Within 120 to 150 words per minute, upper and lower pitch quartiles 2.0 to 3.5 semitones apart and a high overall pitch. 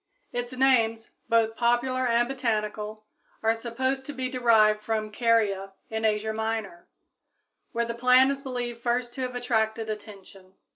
Yes: average, 145 wpm; narrow, 2.4 semitones; high, 230 Hz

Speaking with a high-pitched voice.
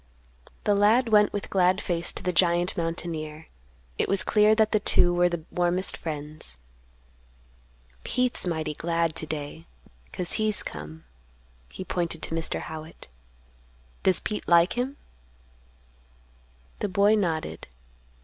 No: medium, 175 Hz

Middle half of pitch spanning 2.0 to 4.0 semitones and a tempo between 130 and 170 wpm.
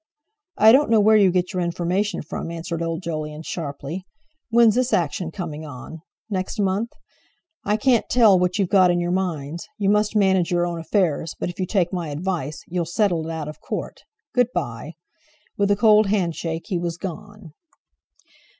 No: average, 3.7 semitones; average, 180 wpm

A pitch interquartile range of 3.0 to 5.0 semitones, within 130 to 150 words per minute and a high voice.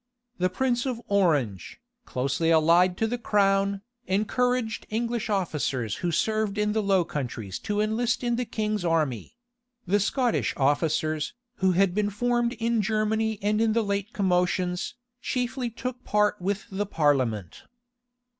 Yes: average, 4.4 semitones; average, 145 wpm; high, 205 Hz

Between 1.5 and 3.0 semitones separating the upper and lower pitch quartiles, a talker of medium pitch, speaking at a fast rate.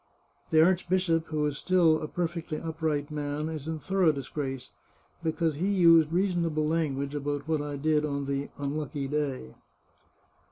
No: narrow, 2.4 semitones; medium, 155 Hz; average, 160 wpm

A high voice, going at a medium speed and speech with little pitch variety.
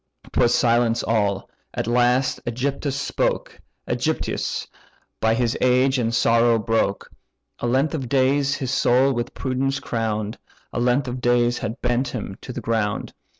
No: low, 120 Hz; average, 150 wpm; narrow, 2.2 semitones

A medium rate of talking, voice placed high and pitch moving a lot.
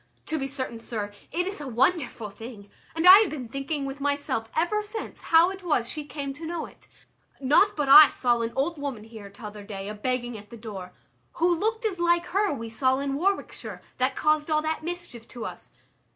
No: fast, 210 wpm; very high, 280 Hz; wide, 6.4 semitones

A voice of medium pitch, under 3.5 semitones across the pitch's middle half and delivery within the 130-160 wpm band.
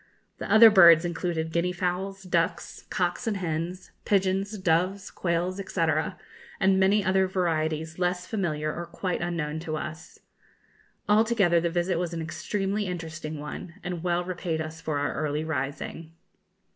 Yes: medium, 175 Hz; average, 2.8 semitones; average, 145 wpm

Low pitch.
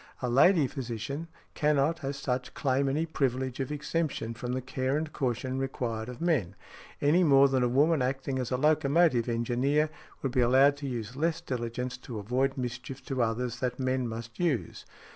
Yes: low, 130 Hz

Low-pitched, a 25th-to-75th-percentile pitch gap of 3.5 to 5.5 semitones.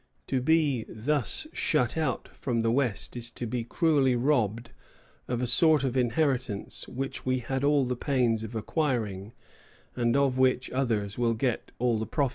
No: low, 125 Hz; average, 2.9 semitones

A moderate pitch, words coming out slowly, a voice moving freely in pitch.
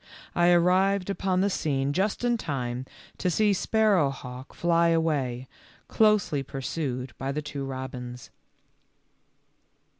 Yes: medium, 155 Hz; slow, 115 wpm; wide, 5.9 semitones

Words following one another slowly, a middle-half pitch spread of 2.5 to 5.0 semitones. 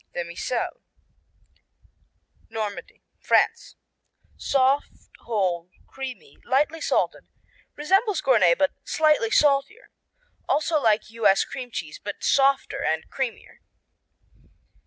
No: slow, 95 wpm; wide, 5.5 semitones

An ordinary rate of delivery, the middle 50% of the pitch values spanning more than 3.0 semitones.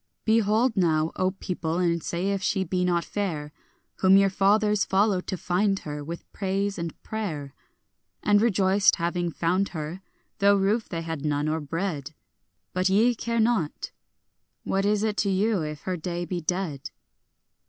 Yes: average, 165 wpm; average, 3.4 semitones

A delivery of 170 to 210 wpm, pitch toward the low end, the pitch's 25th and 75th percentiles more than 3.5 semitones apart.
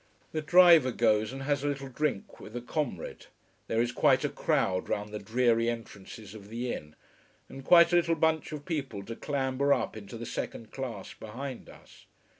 Yes: average, 190 wpm; low, 125 Hz; average, 4.7 semitones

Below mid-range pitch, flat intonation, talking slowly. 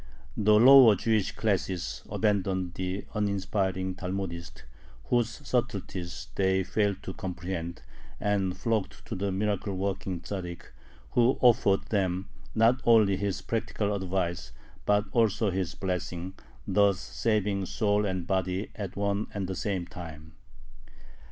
Yes: very low, 95 Hz; narrow, 2.2 semitones; slow, 125 wpm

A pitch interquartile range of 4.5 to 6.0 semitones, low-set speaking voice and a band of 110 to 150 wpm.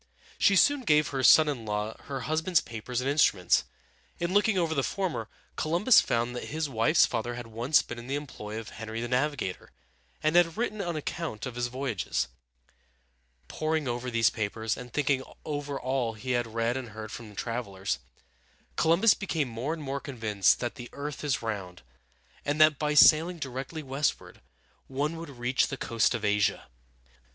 No: average, 5.1 semitones; low, 130 Hz; average, 175 wpm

